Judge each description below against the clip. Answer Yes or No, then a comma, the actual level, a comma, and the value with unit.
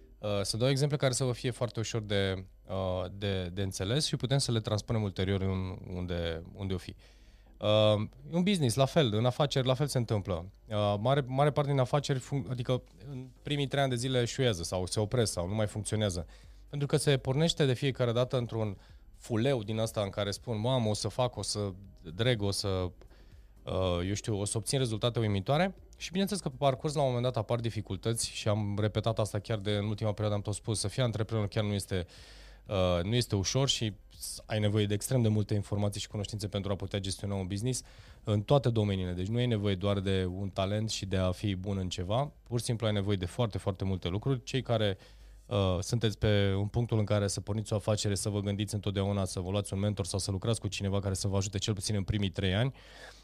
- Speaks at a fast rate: Yes, fast, 225 wpm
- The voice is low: Yes, low, 105 Hz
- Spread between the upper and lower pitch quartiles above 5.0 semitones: No, average, 3.8 semitones